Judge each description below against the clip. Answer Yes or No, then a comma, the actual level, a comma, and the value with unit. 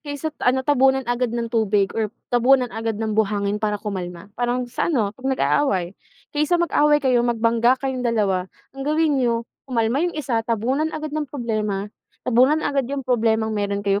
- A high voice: Yes, high, 240 Hz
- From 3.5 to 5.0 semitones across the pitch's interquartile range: Yes, average, 3.8 semitones